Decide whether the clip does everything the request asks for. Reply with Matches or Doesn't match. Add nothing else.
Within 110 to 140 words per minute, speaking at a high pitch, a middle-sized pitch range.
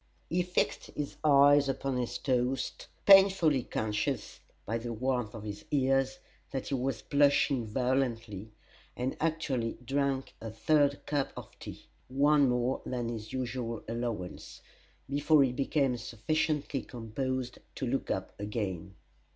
Doesn't match